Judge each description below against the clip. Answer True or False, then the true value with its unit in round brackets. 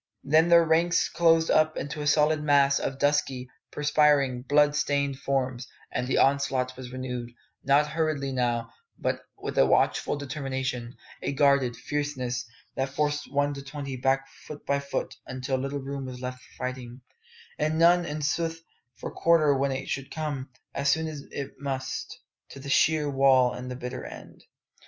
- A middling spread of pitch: False (2.3 semitones)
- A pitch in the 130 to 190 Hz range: True (140 Hz)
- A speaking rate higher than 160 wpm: True (170 wpm)